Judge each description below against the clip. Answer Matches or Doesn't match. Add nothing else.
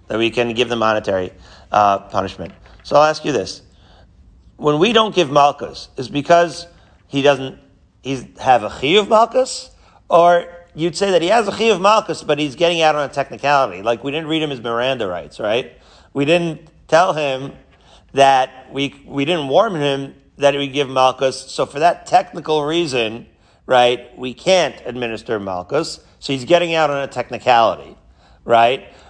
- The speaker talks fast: Doesn't match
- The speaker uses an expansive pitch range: Matches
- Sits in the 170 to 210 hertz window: Doesn't match